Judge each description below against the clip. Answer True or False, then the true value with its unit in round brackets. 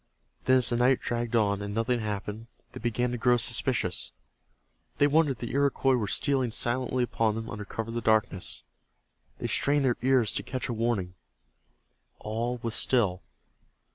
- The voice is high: False (120 Hz)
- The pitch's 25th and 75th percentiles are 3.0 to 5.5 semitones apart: False (2.6 semitones)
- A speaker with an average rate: True (170 wpm)